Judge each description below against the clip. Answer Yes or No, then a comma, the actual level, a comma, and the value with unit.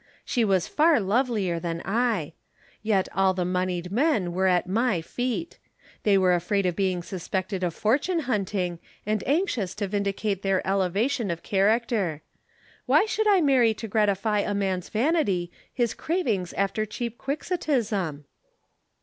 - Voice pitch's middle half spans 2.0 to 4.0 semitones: No, average, 4.5 semitones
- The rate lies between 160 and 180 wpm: No, average, 145 wpm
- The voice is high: Yes, high, 200 Hz